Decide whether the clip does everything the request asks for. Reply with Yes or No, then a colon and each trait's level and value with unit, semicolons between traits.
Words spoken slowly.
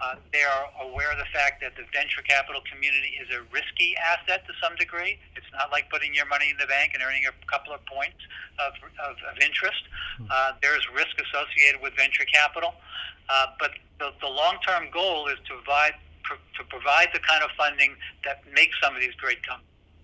No: fast, 205 wpm